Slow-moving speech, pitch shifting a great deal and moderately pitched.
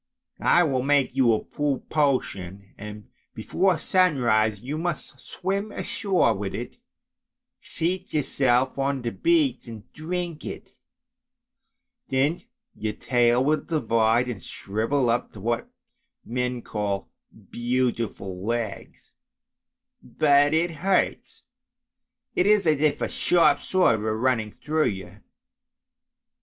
No: slow, 115 wpm; wide, 5.9 semitones; low, 130 Hz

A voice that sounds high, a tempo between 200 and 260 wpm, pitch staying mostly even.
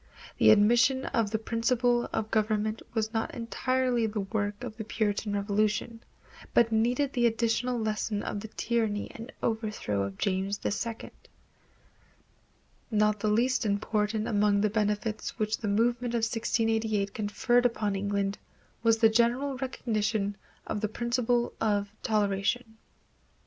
No: high, 220 Hz; slow, 135 wpm; narrow, 2.2 semitones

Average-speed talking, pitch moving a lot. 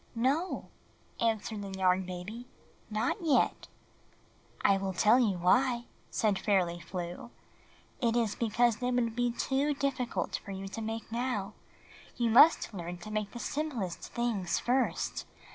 No: average, 145 wpm; average, 4.2 semitones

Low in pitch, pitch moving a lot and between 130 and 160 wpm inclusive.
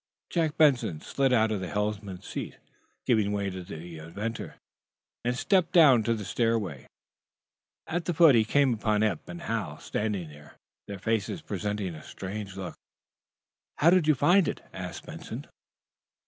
Yes: low, 110 Hz; wide, 5.8 semitones; average, 155 wpm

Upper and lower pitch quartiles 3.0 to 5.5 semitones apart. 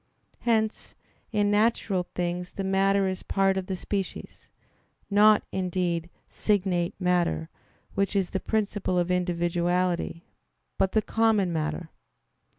No: narrow, 2.4 semitones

